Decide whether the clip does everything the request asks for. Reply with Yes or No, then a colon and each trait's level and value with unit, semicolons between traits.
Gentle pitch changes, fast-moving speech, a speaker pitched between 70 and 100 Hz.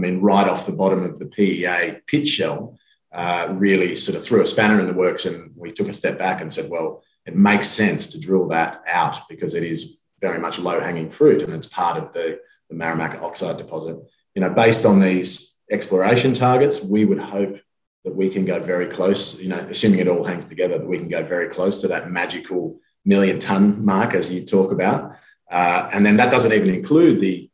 Yes: narrow, 2.3 semitones; fast, 220 wpm; very low, 95 Hz